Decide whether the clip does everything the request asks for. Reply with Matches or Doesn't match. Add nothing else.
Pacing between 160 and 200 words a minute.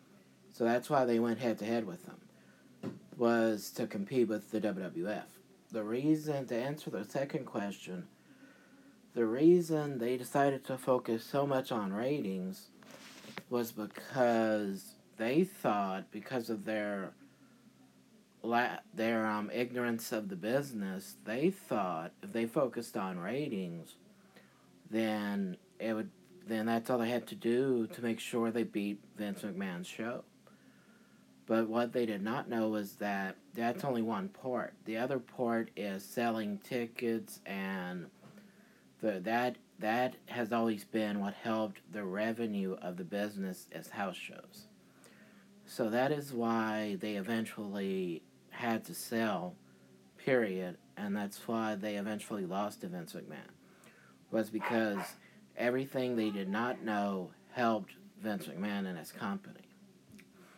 Doesn't match